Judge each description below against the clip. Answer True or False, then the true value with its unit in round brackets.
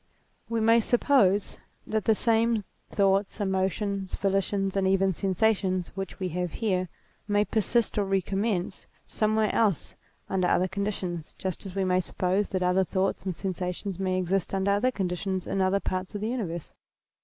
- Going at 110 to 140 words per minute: False (160 wpm)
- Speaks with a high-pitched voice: True (195 Hz)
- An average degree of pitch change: False (2.0 semitones)